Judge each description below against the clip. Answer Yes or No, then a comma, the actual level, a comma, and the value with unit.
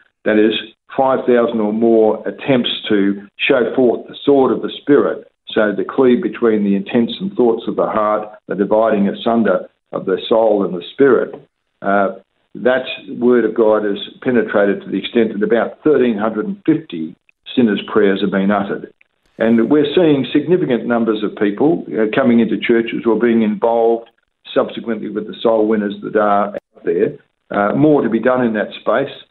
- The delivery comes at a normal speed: Yes, average, 170 wpm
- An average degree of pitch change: No, narrow, 2.2 semitones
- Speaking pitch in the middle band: No, low, 115 Hz